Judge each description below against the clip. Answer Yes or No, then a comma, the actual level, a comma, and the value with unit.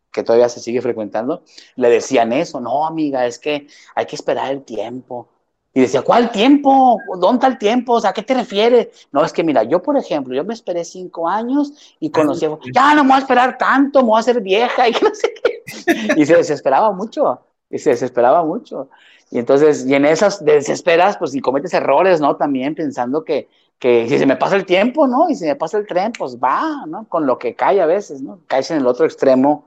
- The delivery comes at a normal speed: No, fast, 225 wpm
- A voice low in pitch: No, high, 225 Hz